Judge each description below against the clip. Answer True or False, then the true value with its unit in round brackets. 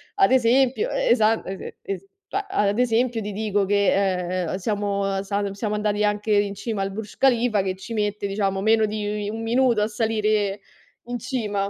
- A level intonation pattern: True (2.2 semitones)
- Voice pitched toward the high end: True (210 Hz)